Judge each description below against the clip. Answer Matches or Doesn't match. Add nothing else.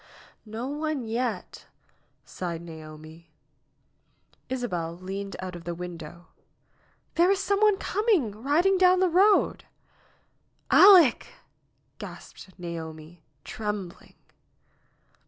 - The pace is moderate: Doesn't match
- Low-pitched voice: Doesn't match